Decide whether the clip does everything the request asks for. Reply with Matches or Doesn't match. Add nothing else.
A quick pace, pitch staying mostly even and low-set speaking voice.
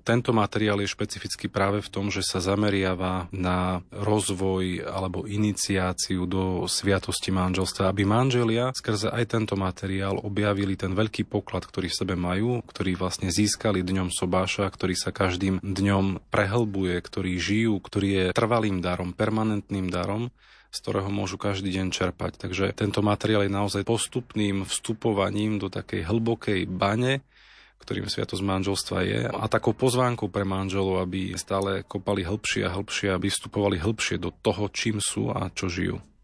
Doesn't match